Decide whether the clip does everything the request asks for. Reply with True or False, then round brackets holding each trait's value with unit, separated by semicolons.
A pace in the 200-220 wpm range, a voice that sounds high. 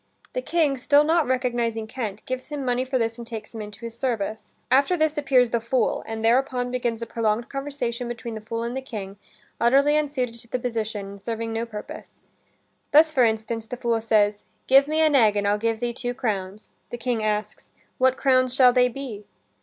True (205 wpm; 240 Hz)